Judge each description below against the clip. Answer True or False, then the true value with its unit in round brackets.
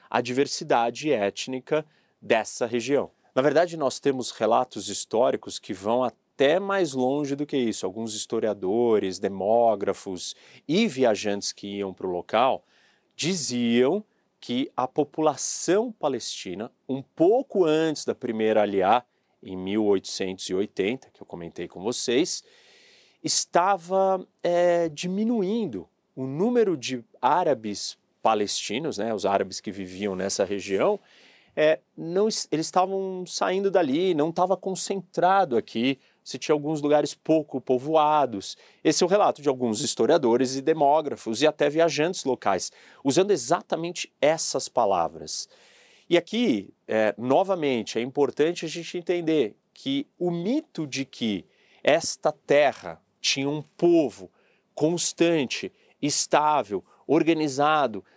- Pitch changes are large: True (7.1 semitones)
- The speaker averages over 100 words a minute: True (120 wpm)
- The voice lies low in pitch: False (150 Hz)